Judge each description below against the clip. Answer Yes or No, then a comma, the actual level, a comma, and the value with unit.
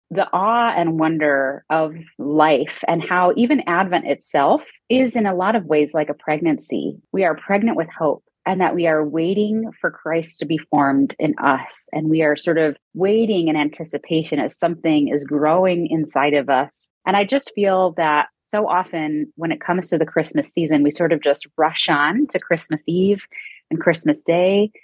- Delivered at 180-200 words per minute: Yes, average, 190 wpm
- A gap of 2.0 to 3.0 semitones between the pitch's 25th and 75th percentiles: No, average, 3.8 semitones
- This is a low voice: No, medium, 165 Hz